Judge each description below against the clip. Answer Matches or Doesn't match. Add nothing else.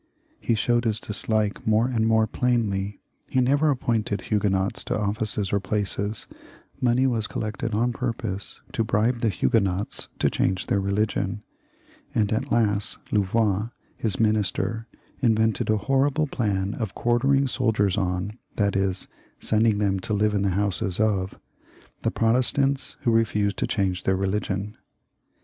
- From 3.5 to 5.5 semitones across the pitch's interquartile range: Doesn't match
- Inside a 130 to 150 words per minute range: Matches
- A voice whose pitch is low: Matches